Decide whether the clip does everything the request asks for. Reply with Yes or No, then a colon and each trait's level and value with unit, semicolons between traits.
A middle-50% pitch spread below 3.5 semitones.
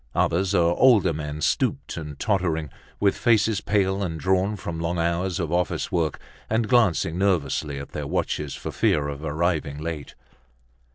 No: average, 4.1 semitones